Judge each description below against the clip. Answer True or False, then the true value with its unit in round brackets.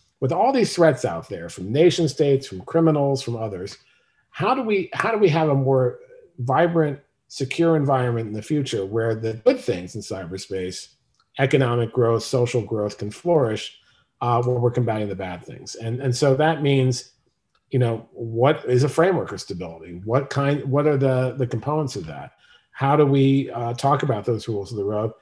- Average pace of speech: True (190 wpm)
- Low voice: True (130 Hz)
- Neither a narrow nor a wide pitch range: True (4.2 semitones)